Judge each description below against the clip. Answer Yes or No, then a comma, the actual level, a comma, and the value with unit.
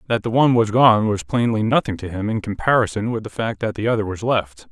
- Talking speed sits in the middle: No, fast, 255 wpm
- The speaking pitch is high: No, low, 110 Hz